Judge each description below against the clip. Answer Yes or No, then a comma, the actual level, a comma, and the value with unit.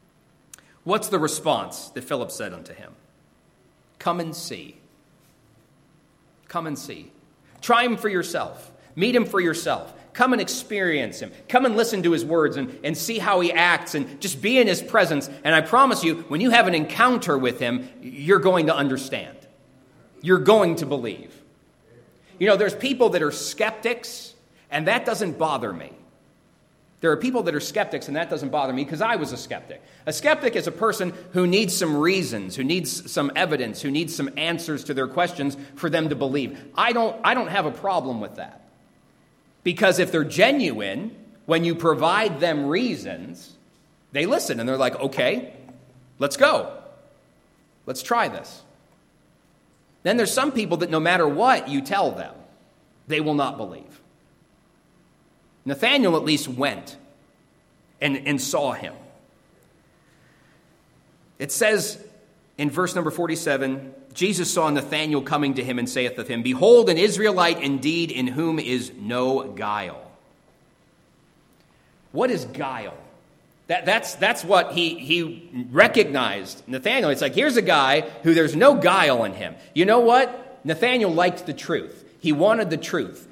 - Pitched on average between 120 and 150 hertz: No, medium, 165 Hz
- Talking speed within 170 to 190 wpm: No, average, 160 wpm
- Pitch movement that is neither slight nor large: No, wide, 6.2 semitones